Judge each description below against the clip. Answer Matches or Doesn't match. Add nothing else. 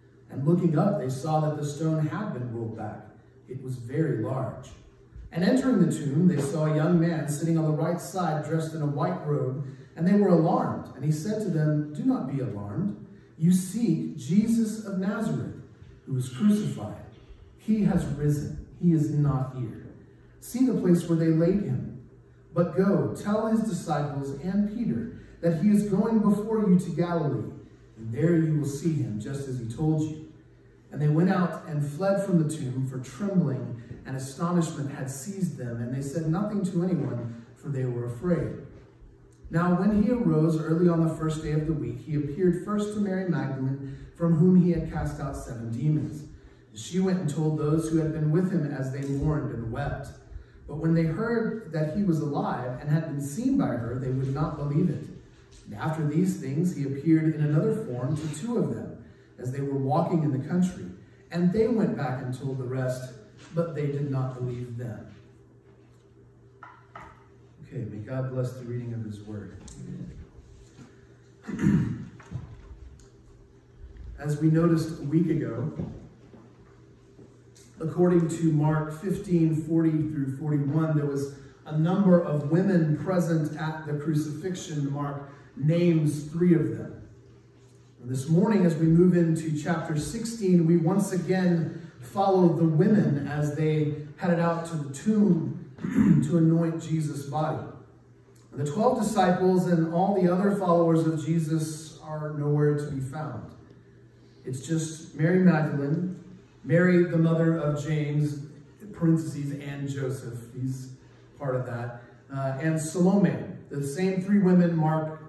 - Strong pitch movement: Doesn't match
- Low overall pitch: Doesn't match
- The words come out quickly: Doesn't match